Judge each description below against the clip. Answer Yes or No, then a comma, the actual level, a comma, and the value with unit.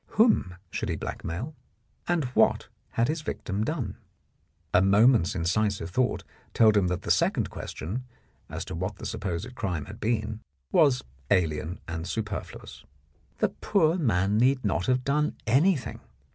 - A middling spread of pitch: No, wide, 6.1 semitones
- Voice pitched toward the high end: No, low, 110 Hz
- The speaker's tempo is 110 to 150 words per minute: Yes, average, 145 wpm